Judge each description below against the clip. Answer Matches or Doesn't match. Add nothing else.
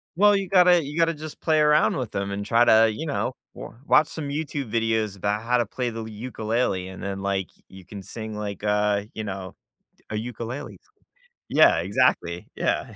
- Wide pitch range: Matches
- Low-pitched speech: Matches